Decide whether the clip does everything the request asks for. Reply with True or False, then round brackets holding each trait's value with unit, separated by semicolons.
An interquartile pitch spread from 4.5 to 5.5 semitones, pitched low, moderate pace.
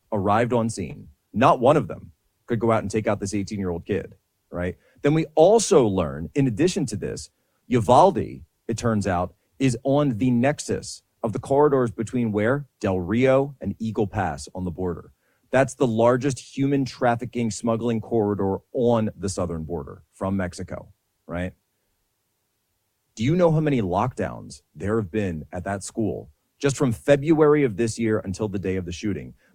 True (5.1 semitones; 110 Hz; 175 wpm)